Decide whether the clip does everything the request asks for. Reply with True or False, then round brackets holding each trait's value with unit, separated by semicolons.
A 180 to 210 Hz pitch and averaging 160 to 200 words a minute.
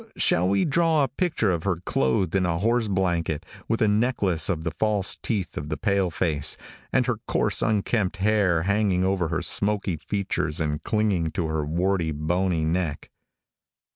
False (95 Hz; 170 wpm)